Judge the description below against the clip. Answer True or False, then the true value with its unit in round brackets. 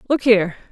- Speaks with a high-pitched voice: True (220 Hz)